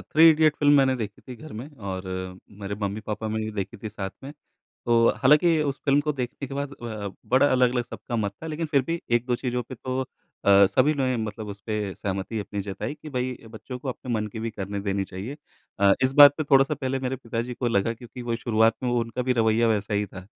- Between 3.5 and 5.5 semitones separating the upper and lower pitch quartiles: Yes, average, 3.9 semitones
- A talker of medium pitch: No, low, 120 Hz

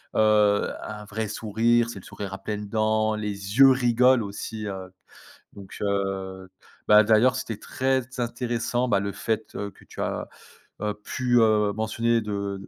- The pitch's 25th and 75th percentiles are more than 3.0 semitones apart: No, narrow, 2.5 semitones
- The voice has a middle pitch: No, low, 110 Hz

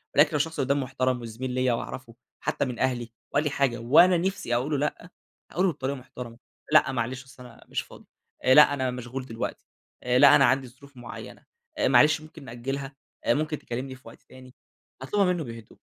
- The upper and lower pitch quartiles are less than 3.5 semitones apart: Yes, average, 2.7 semitones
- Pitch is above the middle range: No, low, 130 Hz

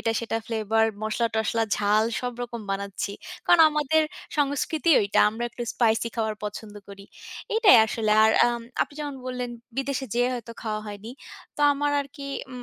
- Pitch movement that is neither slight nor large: Yes, average, 3.7 semitones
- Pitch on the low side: No, high, 235 Hz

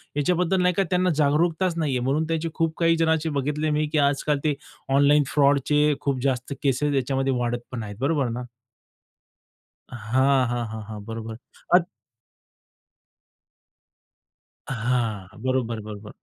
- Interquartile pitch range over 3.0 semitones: Yes, average, 4.1 semitones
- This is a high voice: No, medium, 140 Hz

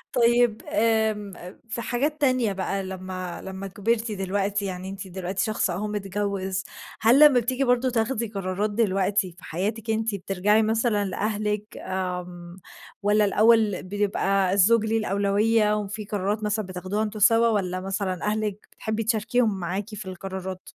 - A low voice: No, high, 205 Hz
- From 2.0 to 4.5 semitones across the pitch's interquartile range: Yes, narrow, 2.6 semitones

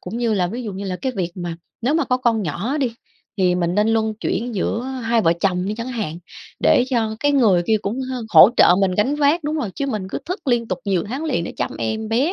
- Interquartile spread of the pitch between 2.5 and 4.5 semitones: No, average, 5.1 semitones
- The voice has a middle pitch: No, high, 225 Hz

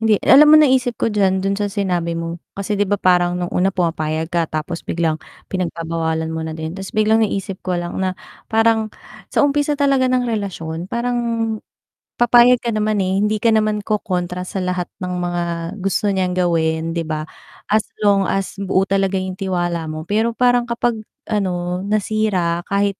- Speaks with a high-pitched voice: Yes, high, 195 Hz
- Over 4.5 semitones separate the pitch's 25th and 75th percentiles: No, average, 3.8 semitones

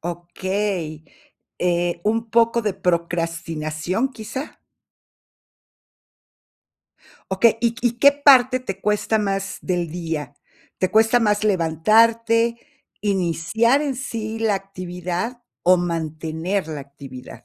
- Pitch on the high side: Yes, high, 195 Hz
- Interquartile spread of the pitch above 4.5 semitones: Yes, average, 5.2 semitones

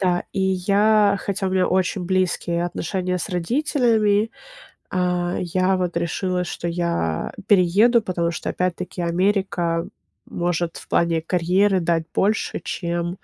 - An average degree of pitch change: No, narrow, 2.3 semitones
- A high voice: No, medium, 180 Hz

